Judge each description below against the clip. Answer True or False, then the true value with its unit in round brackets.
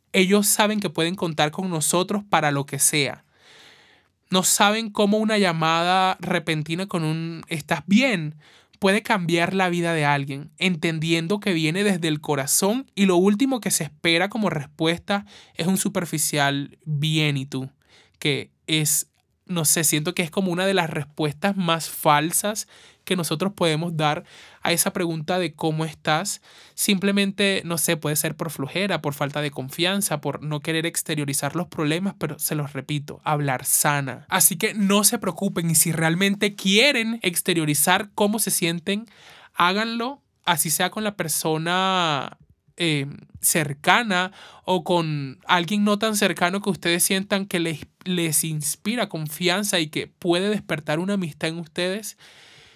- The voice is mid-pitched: True (175 Hz)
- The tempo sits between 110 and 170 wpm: True (155 wpm)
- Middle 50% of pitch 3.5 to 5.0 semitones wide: True (3.8 semitones)